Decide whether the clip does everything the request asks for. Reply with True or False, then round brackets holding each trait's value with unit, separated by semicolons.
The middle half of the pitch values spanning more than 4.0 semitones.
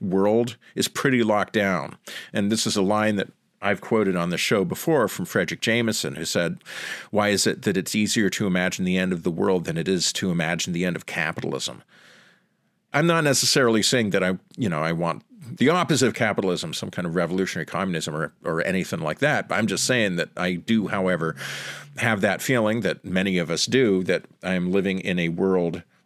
False (3.5 semitones)